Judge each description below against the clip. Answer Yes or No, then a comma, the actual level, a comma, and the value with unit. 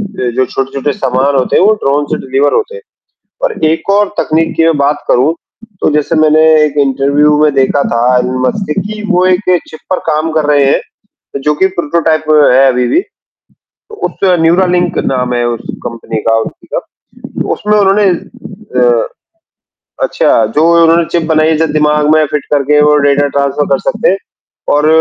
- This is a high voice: No, medium, 150 Hz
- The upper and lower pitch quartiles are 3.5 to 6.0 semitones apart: Yes, average, 4.0 semitones